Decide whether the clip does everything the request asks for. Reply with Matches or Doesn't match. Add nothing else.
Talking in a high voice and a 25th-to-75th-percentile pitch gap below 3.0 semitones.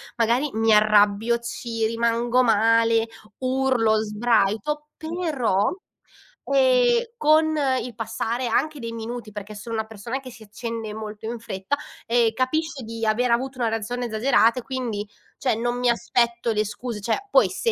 Matches